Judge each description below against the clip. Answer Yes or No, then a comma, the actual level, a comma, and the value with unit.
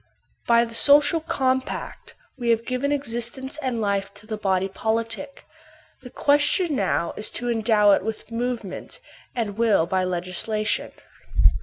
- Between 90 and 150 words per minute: Yes, average, 140 wpm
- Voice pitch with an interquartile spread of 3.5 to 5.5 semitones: Yes, average, 4.0 semitones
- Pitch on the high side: Yes, high, 230 Hz